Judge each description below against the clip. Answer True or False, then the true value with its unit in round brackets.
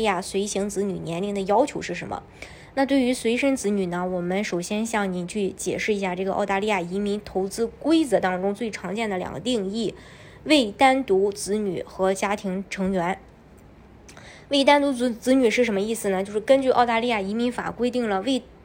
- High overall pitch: True (205 Hz)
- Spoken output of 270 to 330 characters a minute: True (295 characters per minute)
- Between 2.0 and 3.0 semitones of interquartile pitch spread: False (4.0 semitones)